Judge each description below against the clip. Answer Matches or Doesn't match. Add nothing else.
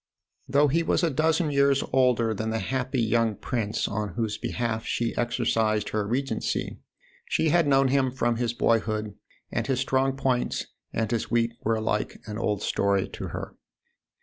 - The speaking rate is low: Doesn't match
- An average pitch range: Matches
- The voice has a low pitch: Matches